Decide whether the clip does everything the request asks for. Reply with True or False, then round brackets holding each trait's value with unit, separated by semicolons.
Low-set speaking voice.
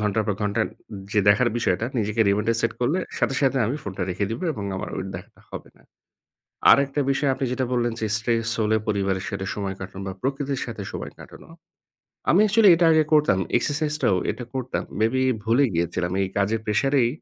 True (115 Hz)